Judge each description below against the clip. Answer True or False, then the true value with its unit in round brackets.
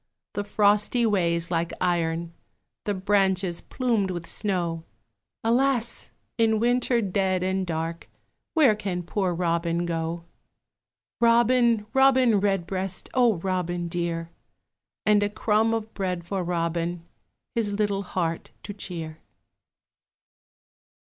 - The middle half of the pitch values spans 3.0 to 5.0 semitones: True (4.0 semitones)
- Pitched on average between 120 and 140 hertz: False (190 Hz)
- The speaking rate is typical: False (110 wpm)